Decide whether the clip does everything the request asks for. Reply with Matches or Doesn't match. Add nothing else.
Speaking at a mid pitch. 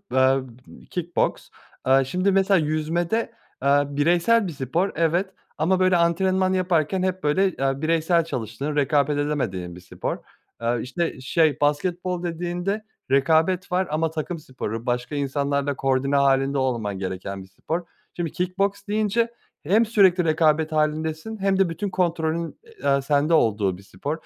Matches